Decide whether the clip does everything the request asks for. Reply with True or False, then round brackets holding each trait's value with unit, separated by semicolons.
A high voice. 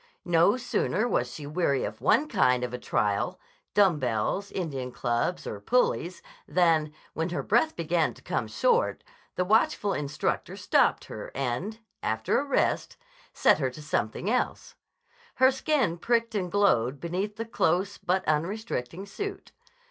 False (175 Hz)